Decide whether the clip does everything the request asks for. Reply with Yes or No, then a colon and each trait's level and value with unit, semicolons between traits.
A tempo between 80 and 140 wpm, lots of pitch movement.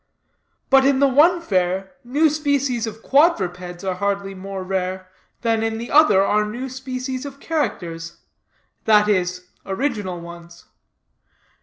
Yes: slow, 135 wpm; wide, 6.2 semitones